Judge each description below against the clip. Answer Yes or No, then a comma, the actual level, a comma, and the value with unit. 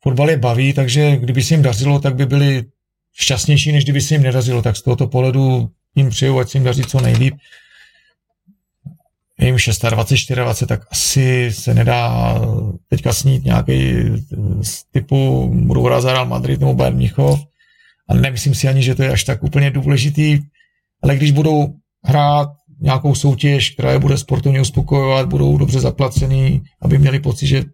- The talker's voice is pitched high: No, low, 135 Hz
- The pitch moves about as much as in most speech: Yes, average, 3.4 semitones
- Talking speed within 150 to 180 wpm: Yes, average, 165 wpm